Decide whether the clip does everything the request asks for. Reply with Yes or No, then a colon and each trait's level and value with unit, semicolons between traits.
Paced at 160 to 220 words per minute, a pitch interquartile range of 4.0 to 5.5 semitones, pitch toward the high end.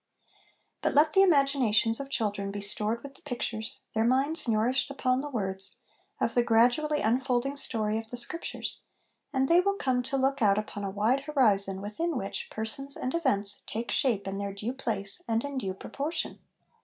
Yes: average, 180 wpm; average, 4.7 semitones; high, 240 Hz